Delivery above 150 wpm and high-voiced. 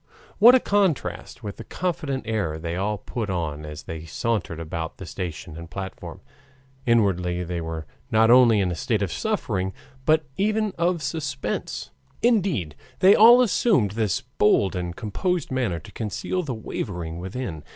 No: average, 160 wpm; low, 105 Hz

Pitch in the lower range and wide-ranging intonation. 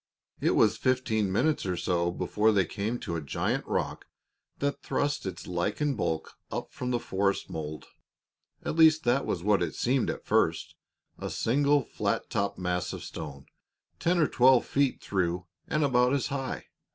Yes: low, 110 Hz; wide, 7.4 semitones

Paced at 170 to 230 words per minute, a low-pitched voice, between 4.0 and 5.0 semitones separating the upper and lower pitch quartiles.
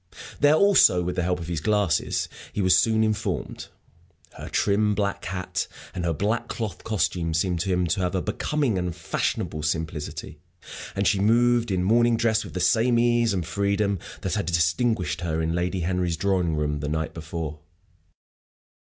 Yes: average, 175 wpm; very low, 95 Hz; average, 4.3 semitones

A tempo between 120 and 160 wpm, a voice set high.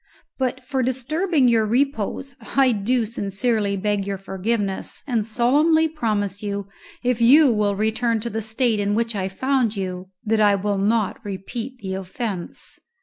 Yes: average, 155 wpm; high, 220 Hz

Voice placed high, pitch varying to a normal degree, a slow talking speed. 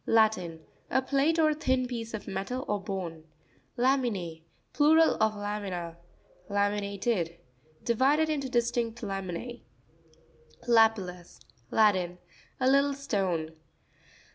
No: high, 215 Hz; wide, 6.0 semitones; slow, 90 wpm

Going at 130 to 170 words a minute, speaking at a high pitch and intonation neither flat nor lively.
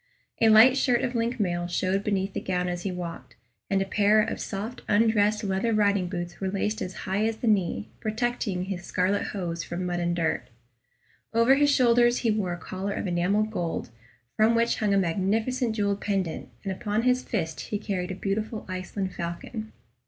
No: average, 190 wpm; high, 200 Hz; average, 3.3 semitones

